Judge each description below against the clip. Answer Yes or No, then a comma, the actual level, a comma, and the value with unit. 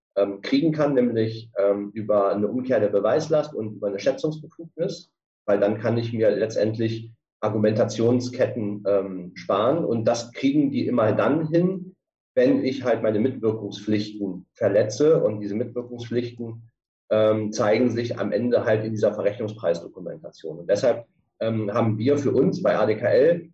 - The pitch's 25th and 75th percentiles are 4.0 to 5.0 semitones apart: No, average, 3.6 semitones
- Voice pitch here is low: Yes, low, 115 Hz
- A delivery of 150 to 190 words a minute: No, average, 135 wpm